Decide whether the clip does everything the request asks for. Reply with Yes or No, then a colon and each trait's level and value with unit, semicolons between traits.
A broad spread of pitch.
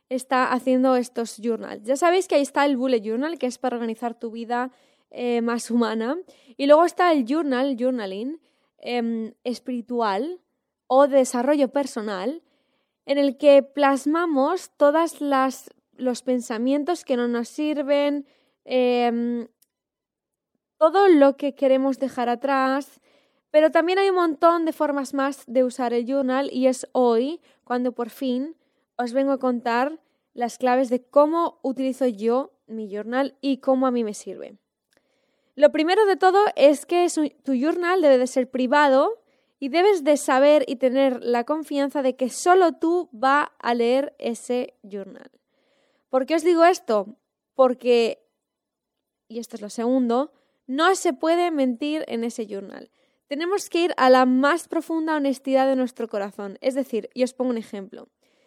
No: average, 3.0 semitones